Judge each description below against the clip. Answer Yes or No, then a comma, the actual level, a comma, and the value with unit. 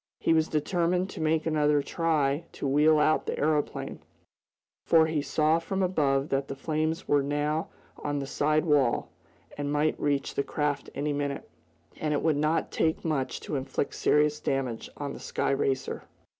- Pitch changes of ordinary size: No, narrow, 1.9 semitones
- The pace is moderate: Yes, average, 170 wpm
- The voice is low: No, medium, 150 Hz